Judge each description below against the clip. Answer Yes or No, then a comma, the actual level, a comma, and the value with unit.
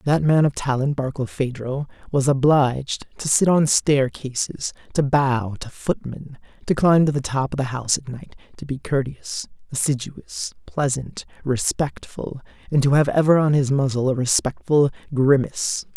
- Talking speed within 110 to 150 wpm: No, average, 160 wpm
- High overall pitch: No, medium, 140 Hz